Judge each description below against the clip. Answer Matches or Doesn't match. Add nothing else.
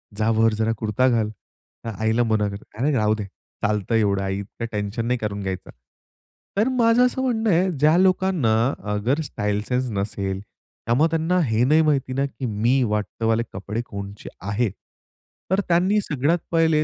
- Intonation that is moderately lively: Doesn't match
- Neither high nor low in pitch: Doesn't match